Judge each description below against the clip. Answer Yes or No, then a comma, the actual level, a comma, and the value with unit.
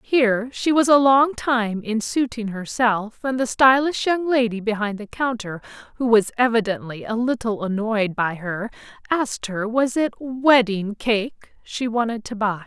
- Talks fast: No, average, 165 wpm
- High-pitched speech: Yes, high, 230 Hz